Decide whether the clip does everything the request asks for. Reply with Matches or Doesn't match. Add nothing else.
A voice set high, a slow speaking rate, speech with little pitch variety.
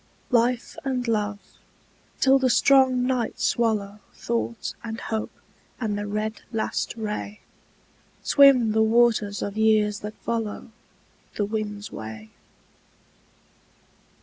Matches